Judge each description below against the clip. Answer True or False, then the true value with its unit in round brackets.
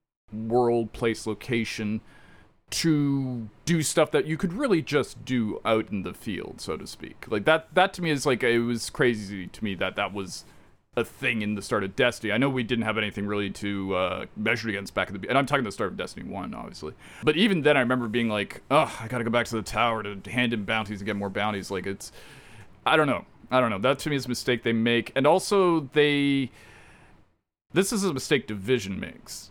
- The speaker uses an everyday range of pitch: True (4.2 semitones)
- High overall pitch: False (115 Hz)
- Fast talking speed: True (230 wpm)